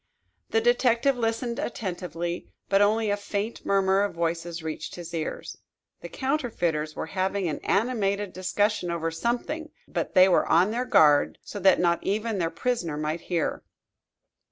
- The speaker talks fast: No, average, 155 wpm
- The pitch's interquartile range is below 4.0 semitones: No, average, 4.8 semitones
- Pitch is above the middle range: Yes, high, 195 Hz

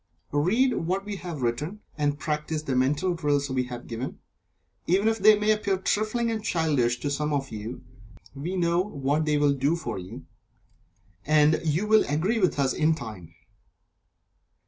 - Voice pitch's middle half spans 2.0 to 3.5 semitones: No, wide, 5.5 semitones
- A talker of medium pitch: Yes, medium, 155 Hz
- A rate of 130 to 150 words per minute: No, average, 170 wpm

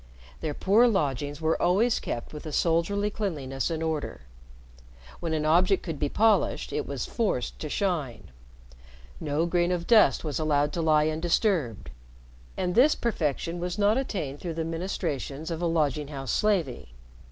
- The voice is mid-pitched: Yes, medium, 165 Hz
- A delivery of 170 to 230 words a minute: No, average, 160 wpm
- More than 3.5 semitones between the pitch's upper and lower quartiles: Yes, average, 4.3 semitones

